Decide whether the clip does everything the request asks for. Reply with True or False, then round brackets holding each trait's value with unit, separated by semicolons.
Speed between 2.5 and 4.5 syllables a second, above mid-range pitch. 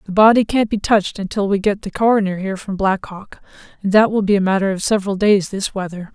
False (6.3 syllables/s; 200 Hz)